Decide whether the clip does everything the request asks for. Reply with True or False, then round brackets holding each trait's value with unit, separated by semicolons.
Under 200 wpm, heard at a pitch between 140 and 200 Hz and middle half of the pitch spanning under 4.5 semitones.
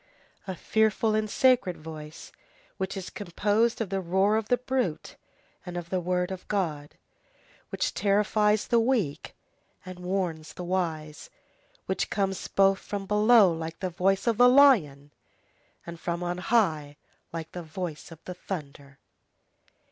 True (150 wpm; 185 Hz; 4.1 semitones)